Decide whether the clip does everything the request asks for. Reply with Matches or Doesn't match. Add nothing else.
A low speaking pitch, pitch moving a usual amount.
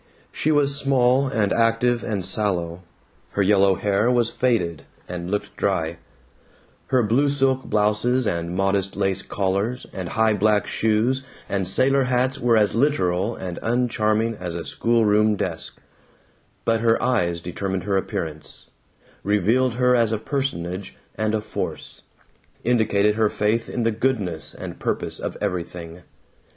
Matches